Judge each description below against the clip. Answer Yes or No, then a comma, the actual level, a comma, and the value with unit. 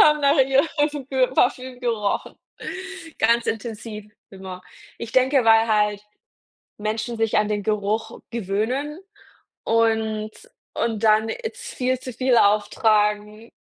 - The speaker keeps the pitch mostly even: No, average, 3.3 semitones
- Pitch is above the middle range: Yes, high, 225 Hz